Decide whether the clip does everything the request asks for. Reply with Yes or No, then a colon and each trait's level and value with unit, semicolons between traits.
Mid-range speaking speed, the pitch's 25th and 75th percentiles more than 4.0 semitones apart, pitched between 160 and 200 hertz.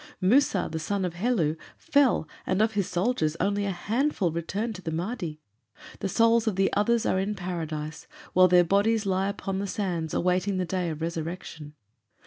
No: average, 180 wpm; average, 3.6 semitones; medium, 185 Hz